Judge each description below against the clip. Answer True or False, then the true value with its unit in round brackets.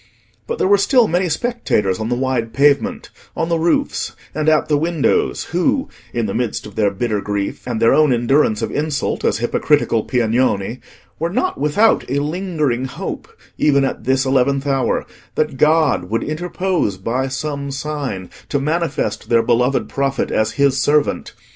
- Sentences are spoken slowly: False (165 wpm)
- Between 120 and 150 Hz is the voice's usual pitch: True (140 Hz)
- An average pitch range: True (4.7 semitones)